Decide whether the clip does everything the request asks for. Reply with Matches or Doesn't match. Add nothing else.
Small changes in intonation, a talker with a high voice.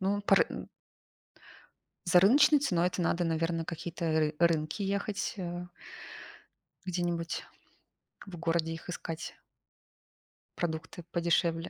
Doesn't match